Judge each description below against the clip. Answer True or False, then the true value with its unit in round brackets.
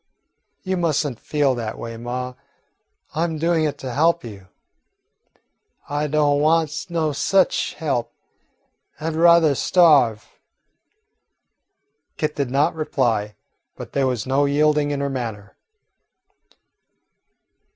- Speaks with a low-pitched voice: False (145 Hz)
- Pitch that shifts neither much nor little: True (4.0 semitones)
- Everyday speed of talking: False (120 wpm)